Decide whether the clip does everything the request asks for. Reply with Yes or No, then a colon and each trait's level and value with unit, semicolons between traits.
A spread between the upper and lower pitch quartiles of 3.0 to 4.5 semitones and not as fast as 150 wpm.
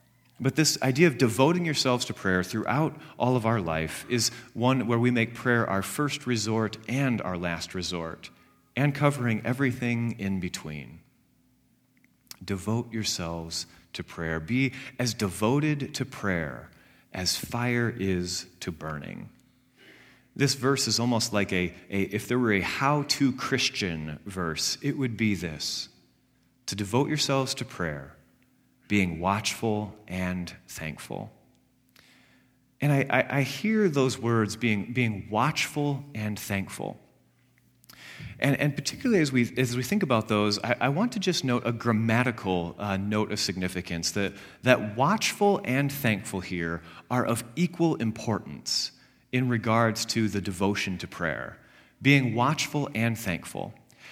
No: wide, 5.5 semitones; average, 140 wpm